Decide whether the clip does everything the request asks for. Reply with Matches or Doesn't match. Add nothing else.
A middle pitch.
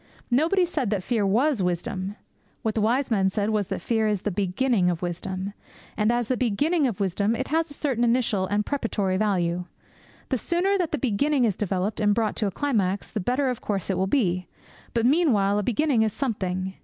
Doesn't match